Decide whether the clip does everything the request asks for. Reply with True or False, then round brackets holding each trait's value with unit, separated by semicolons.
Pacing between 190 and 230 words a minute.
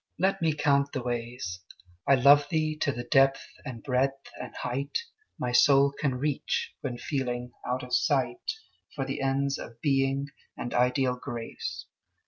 False (155 wpm)